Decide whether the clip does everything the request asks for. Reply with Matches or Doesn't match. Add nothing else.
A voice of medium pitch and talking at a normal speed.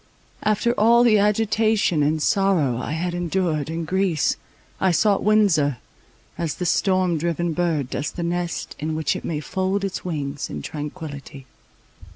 Matches